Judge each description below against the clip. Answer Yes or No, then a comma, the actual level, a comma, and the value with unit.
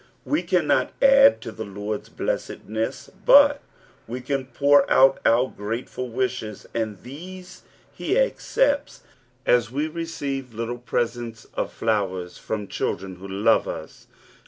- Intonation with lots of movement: Yes, wide, 5.7 semitones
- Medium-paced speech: No, slow, 130 wpm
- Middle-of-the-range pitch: No, low, 125 Hz